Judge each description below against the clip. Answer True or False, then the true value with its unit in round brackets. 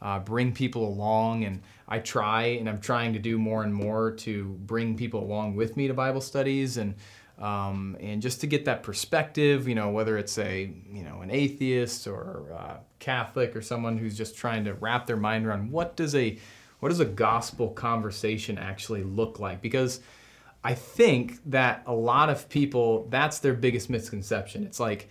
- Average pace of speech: True (190 wpm)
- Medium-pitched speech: False (115 Hz)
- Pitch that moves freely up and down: False (3.1 semitones)